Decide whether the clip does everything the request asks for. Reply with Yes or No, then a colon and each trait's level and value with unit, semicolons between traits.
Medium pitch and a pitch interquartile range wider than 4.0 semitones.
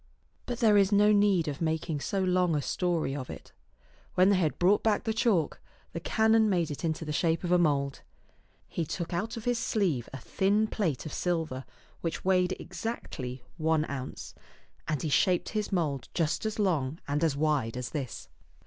Yes: medium, 170 Hz; average, 5.1 semitones